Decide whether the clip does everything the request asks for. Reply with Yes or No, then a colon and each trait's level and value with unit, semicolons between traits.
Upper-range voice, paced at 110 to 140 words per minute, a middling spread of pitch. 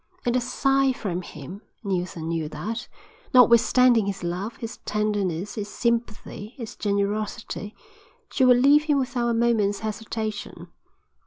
Yes: high, 215 Hz; slow, 135 wpm; average, 3.3 semitones